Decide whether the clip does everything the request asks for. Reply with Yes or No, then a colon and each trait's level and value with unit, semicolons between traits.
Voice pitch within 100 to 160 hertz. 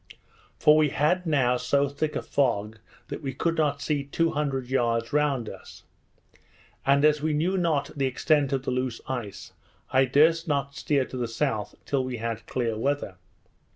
Yes: medium, 140 Hz